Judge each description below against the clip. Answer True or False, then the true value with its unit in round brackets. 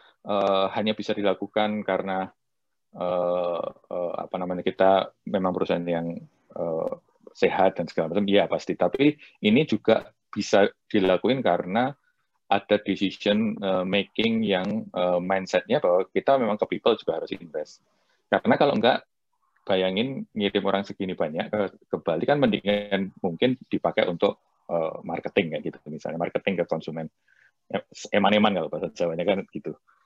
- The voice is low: True (100 Hz)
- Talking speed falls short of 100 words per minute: False (140 wpm)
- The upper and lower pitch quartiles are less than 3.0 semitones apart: True (2.4 semitones)